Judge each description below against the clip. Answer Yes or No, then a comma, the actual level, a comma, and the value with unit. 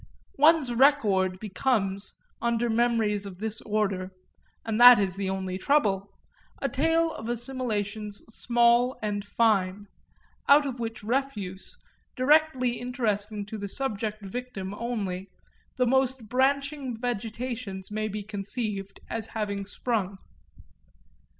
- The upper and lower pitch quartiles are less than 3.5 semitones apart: No, average, 3.8 semitones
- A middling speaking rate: No, slow, 120 wpm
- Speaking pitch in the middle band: No, high, 220 Hz